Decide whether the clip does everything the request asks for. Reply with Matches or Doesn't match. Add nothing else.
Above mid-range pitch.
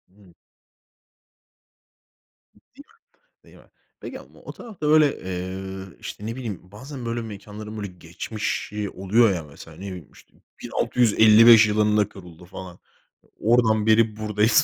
Doesn't match